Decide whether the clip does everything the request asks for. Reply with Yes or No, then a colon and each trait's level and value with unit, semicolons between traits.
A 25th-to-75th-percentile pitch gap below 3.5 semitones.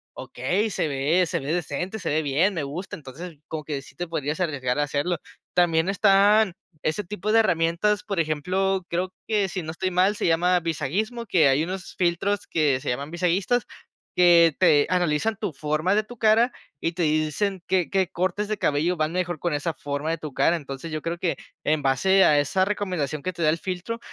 No: average, 3.9 semitones